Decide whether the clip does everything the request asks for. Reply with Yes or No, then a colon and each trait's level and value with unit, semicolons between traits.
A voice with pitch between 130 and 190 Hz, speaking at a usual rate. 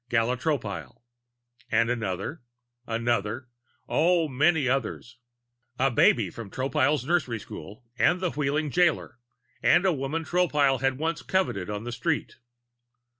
No: low, 135 Hz; slow, 125 wpm